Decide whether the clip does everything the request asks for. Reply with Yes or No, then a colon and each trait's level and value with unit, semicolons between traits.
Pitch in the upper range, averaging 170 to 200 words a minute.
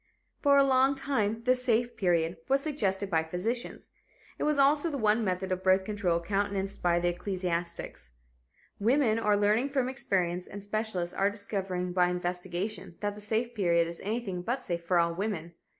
Yes: high, 200 Hz; average, 175 wpm